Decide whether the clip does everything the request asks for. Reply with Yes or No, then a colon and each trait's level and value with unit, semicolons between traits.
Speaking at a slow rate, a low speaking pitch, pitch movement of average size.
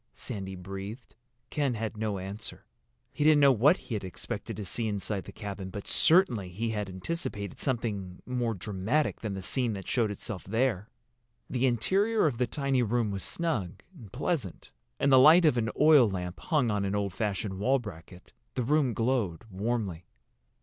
No: average, 175 wpm; low, 110 Hz; average, 5.0 semitones